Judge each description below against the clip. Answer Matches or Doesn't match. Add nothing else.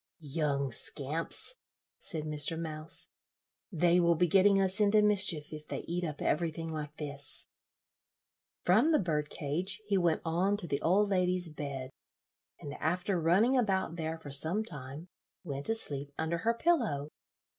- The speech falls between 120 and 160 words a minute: Matches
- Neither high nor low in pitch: Matches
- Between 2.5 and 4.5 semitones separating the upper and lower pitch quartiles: Matches